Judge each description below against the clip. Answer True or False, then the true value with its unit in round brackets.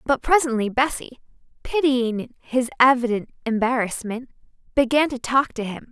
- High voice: True (250 Hz)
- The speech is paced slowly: True (120 wpm)